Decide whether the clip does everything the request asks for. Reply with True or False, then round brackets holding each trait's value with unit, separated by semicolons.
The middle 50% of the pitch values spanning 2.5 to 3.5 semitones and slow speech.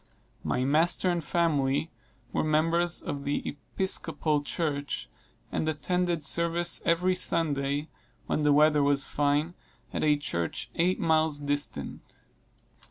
True (2.8 semitones; 120 wpm)